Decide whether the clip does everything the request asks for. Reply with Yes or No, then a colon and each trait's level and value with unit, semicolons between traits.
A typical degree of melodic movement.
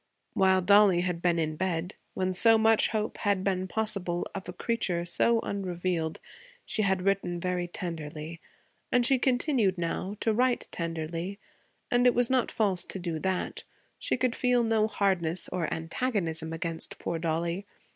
Yes: average, 4.3 semitones